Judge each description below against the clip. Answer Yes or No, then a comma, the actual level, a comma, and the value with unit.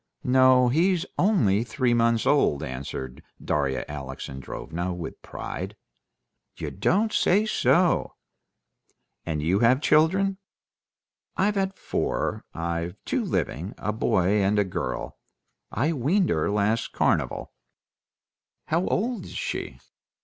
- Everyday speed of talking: No, slow, 115 wpm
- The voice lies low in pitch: Yes, low, 115 Hz